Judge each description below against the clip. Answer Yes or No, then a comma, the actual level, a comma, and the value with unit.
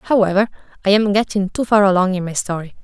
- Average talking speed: No, fast, 210 wpm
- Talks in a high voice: Yes, high, 195 Hz